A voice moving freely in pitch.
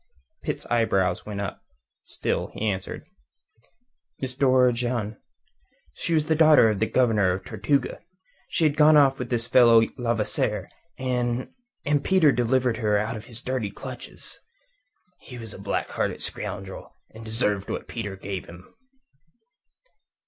No: average, 3.7 semitones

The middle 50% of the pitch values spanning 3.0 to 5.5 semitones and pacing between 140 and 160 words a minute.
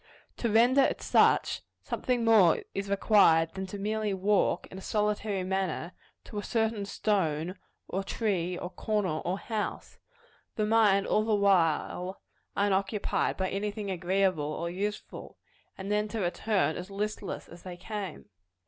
No: narrow, 2.5 semitones; average, 150 wpm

